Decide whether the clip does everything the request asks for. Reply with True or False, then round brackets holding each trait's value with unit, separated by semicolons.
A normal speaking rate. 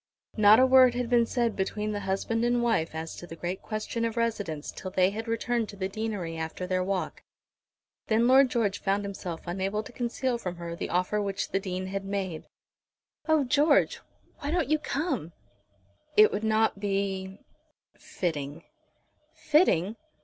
True (170 wpm)